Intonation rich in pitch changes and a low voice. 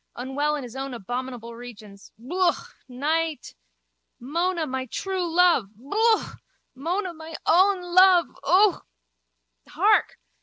No: wide, 6.2 semitones; very high, 310 Hz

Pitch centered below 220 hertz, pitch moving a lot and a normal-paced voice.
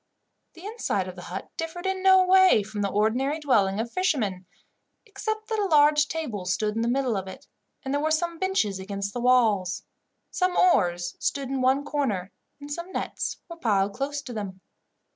No: very high, 265 Hz; wide, 8.8 semitones; average, 190 wpm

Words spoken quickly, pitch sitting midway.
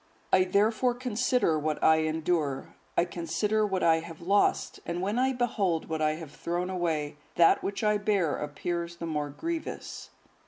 No: average, 165 wpm; medium, 175 Hz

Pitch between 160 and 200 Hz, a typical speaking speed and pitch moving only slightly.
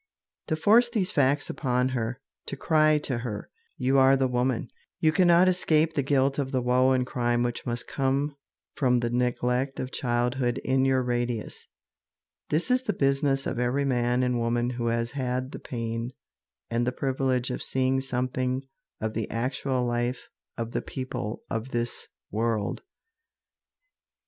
No: low, 130 Hz; average, 160 wpm; narrow, 2.2 semitones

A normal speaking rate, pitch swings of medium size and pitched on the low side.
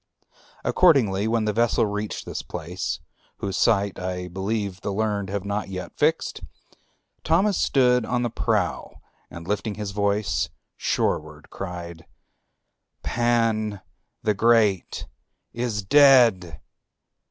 No: slow, 115 wpm; average, 3.4 semitones; low, 105 Hz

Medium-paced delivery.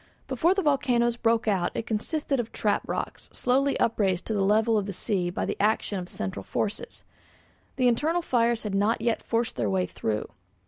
Yes: average, 190 wpm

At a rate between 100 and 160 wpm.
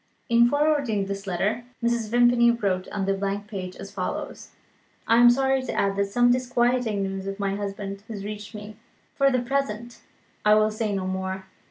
No: average, 185 wpm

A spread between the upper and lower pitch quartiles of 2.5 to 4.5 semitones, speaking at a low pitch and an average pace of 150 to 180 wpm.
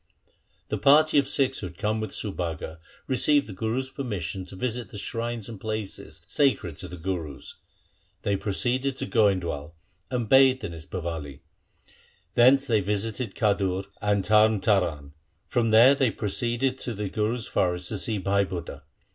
No: average, 4.9 semitones; low, 105 Hz; average, 160 wpm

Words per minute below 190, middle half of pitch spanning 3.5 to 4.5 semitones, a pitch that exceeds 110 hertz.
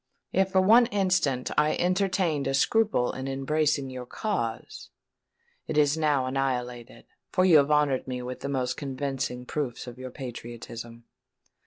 Yes: average, 150 wpm; average, 3.9 semitones; low, 135 Hz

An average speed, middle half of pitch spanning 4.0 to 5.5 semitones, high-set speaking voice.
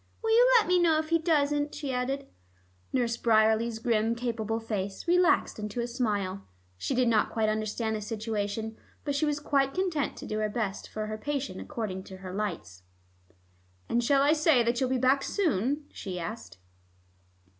Yes: average, 180 wpm; average, 5.1 semitones; high, 235 Hz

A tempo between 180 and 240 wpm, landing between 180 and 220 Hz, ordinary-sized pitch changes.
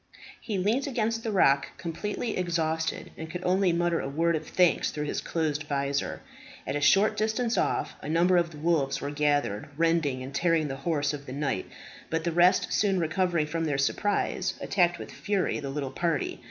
No: average, 195 wpm; medium, 165 Hz; average, 3.9 semitones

